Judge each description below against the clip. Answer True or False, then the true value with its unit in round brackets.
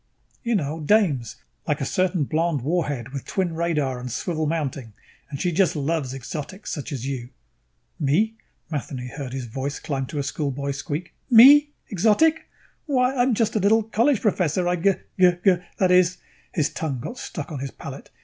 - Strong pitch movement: True (5.9 semitones)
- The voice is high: False (160 Hz)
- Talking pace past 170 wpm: True (180 wpm)